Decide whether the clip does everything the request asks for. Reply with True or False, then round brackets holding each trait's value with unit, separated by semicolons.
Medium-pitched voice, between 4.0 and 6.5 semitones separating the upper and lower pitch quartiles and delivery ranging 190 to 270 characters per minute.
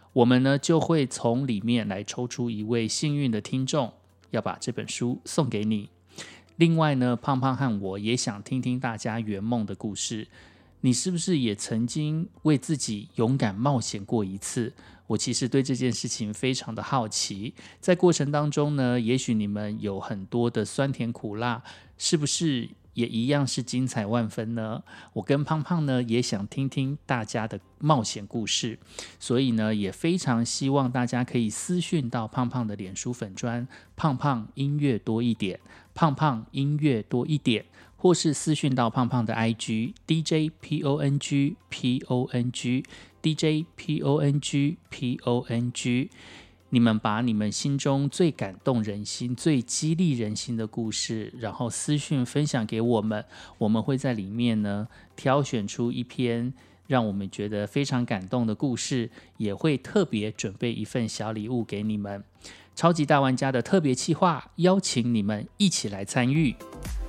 False (120 Hz; 4.4 semitones; 245 characters per minute)